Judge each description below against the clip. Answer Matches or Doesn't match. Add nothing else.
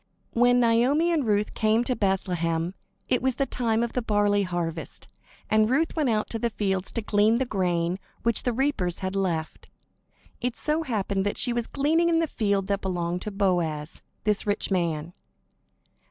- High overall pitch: Matches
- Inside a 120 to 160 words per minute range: Doesn't match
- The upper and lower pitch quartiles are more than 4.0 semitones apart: Matches